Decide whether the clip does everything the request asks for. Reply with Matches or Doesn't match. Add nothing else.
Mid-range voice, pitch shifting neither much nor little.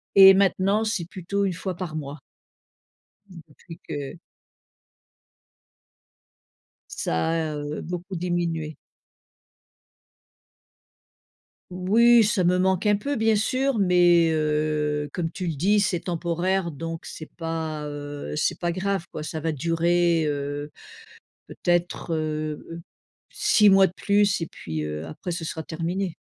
Matches